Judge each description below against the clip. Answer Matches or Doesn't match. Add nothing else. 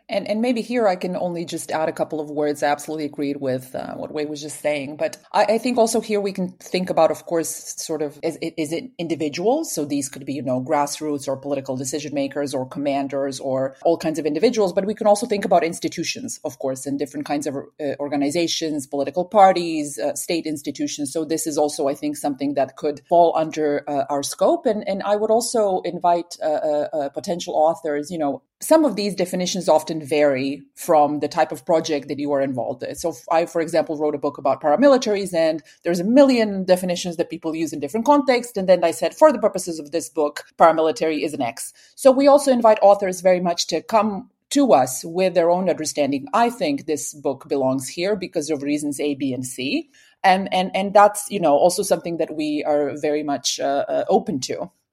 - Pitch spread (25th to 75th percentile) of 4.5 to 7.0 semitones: Matches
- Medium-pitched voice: Matches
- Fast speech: Matches